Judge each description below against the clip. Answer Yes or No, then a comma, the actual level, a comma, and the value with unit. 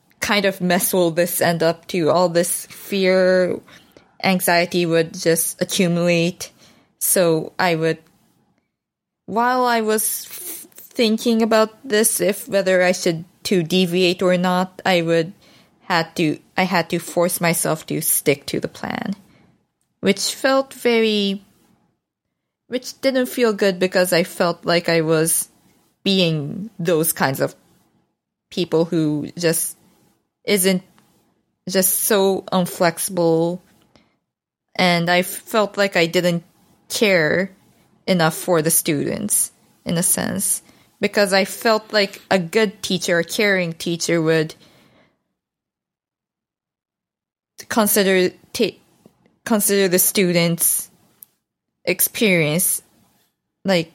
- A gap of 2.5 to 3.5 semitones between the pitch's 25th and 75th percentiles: Yes, average, 2.9 semitones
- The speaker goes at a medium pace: No, slow, 115 wpm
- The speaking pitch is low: No, medium, 185 Hz